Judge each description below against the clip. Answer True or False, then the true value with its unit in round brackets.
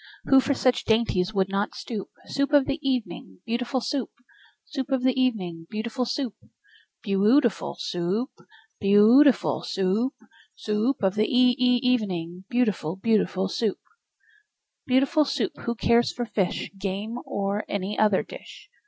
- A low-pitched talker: False (225 Hz)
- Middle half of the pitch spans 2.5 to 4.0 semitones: False (4.5 semitones)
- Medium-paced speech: True (155 wpm)